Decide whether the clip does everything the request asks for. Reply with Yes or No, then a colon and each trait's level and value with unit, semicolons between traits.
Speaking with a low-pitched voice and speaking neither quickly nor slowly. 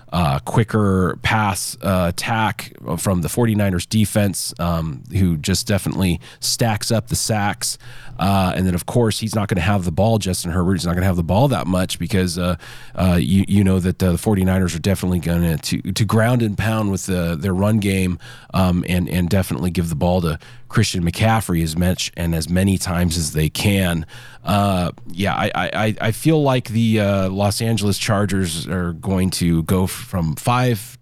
Yes: very low, 95 Hz; average, 195 wpm